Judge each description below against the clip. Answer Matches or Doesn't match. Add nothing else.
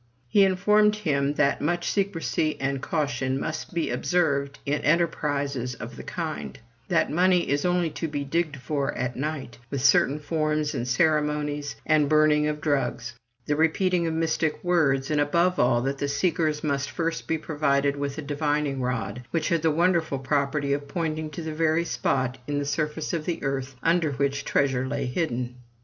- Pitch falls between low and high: Matches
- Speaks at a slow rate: Doesn't match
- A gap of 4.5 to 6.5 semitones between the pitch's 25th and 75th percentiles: Doesn't match